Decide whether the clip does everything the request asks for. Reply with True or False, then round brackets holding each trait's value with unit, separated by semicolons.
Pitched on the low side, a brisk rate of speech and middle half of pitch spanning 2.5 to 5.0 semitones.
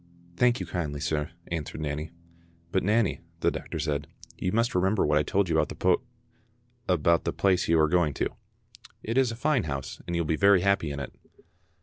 False (90 Hz; 215 wpm; 5.4 semitones)